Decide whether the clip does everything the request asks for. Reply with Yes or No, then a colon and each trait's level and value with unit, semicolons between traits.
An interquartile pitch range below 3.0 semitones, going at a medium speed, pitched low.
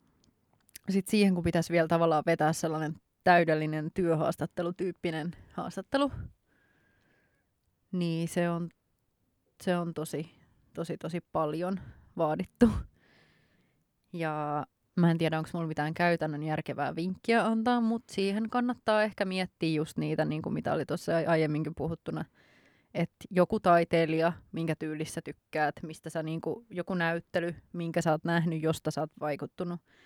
No: narrow, 2.4 semitones; average, 130 wpm; medium, 170 Hz